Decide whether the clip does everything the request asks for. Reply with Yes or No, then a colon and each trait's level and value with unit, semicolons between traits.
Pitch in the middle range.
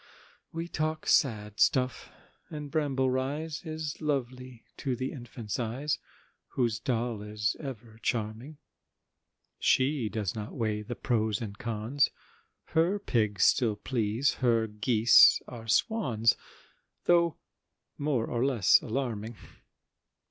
No: low, 120 Hz